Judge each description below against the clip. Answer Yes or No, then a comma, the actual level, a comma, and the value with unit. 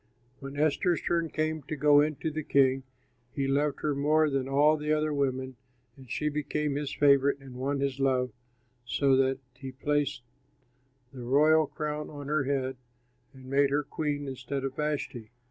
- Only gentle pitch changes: Yes, narrow, 2.0 semitones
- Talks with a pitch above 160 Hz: No, medium, 140 Hz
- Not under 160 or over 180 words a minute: Yes, average, 175 wpm